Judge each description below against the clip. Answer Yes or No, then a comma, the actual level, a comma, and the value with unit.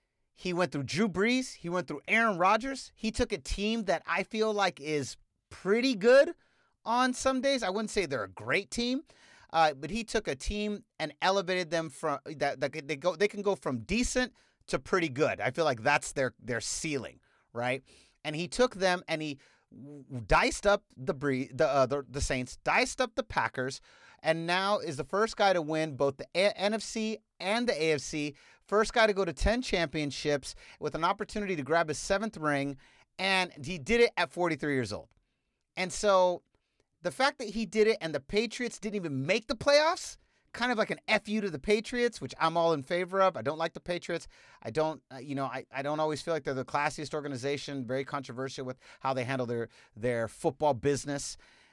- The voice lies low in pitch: No, medium, 175 Hz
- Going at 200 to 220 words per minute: Yes, fast, 205 wpm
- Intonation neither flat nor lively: No, wide, 6.9 semitones